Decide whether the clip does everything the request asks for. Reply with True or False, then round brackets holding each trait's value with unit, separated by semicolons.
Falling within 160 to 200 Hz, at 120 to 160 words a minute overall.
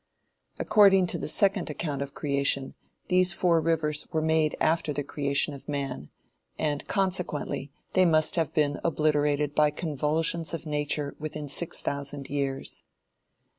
False (150 Hz; 140 wpm)